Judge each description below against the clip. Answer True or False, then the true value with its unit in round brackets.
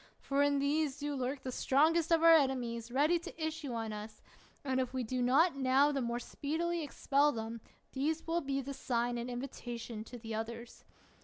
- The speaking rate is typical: True (190 wpm)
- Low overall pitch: False (265 Hz)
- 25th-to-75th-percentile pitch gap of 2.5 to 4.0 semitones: True (3.6 semitones)